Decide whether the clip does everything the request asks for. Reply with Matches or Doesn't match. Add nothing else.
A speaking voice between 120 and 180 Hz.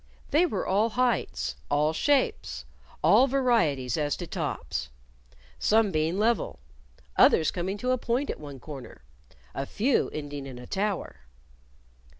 Doesn't match